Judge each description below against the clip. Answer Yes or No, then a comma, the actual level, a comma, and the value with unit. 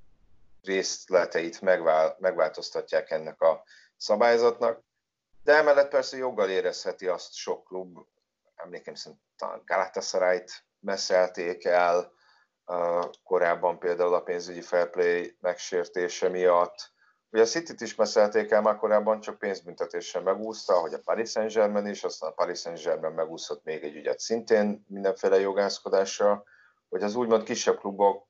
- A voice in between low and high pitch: No, low, 115 Hz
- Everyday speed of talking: Yes, average, 125 wpm